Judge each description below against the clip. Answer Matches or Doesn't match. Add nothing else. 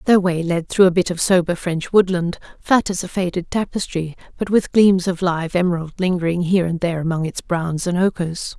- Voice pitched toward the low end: Doesn't match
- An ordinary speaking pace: Doesn't match